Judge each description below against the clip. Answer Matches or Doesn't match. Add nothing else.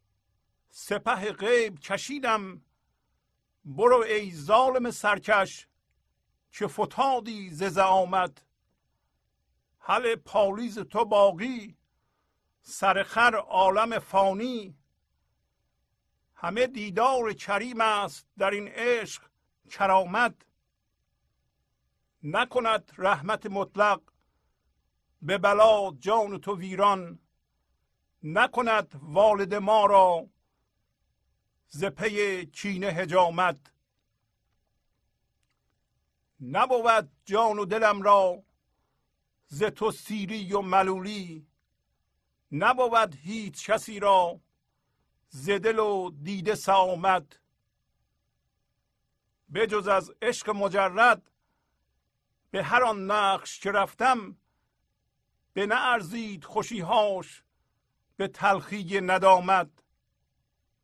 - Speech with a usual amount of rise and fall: Matches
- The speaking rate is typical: Doesn't match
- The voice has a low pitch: Doesn't match